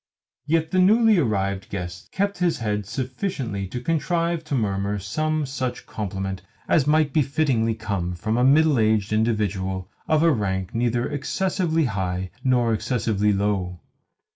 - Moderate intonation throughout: No, wide, 7.7 semitones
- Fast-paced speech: No, average, 140 wpm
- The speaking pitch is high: No, low, 115 Hz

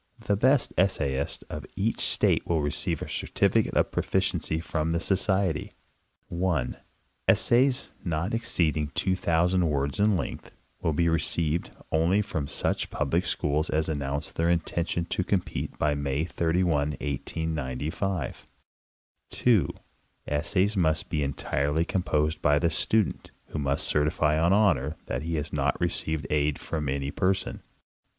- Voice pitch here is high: No, very low, 80 Hz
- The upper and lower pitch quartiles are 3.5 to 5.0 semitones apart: Yes, average, 3.8 semitones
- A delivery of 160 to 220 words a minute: No, average, 145 wpm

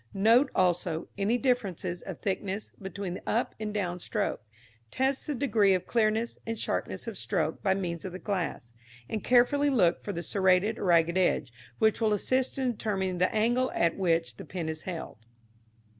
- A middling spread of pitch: Yes, average, 4.2 semitones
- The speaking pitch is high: Yes, high, 195 Hz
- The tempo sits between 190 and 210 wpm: No, average, 180 wpm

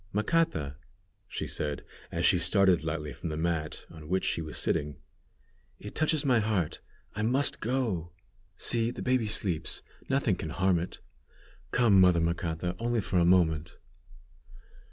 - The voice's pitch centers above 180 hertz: No, very low, 90 Hz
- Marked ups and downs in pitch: Yes, wide, 5.8 semitones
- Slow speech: No, average, 150 wpm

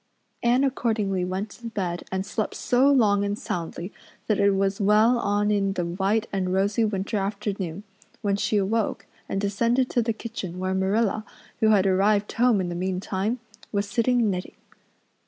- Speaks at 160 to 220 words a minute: Yes, average, 170 wpm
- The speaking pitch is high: Yes, high, 200 Hz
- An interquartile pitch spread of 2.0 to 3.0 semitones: Yes, narrow, 2.5 semitones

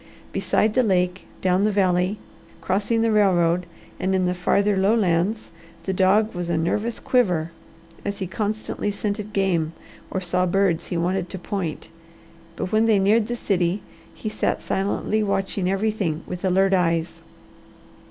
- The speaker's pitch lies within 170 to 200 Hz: Yes, high, 190 Hz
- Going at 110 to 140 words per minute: No, average, 150 wpm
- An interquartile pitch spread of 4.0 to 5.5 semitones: No, average, 2.7 semitones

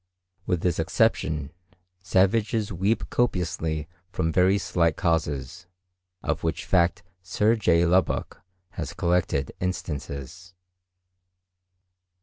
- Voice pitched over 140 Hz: No, very low, 90 Hz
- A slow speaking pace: Yes, slow, 95 wpm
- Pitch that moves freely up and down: No, narrow, 2.6 semitones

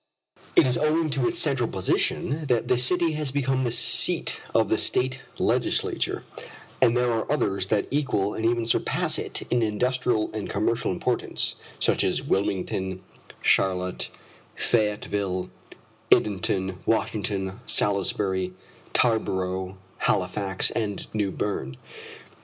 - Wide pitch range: No, average, 4.6 semitones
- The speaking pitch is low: Yes, low, 105 Hz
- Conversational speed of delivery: No, slow, 125 wpm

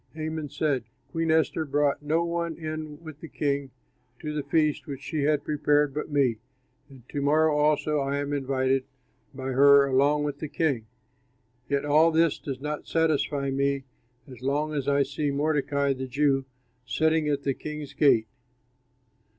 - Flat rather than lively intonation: Yes, narrow, 1.9 semitones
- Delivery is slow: No, average, 165 wpm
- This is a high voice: No, medium, 145 Hz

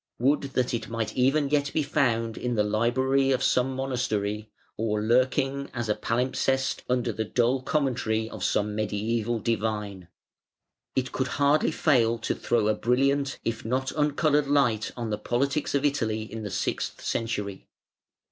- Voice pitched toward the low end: Yes, low, 120 Hz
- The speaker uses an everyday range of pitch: Yes, average, 3.5 semitones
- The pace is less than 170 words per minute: Yes, average, 155 wpm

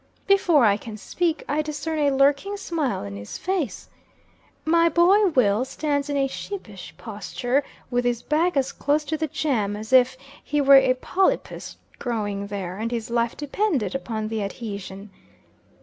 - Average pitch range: No, wide, 6.1 semitones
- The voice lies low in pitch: No, very high, 265 Hz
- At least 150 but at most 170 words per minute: Yes, average, 165 wpm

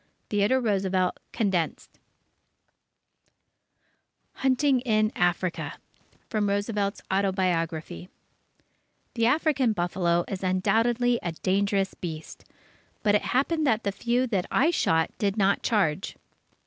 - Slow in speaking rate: Yes, slow, 105 wpm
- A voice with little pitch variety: No, average, 4.2 semitones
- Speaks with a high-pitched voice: Yes, high, 200 Hz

